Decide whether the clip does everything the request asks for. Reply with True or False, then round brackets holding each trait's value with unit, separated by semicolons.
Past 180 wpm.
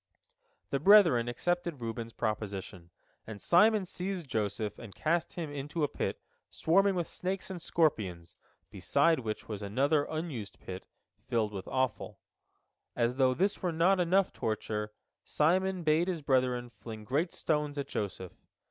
False (150 wpm)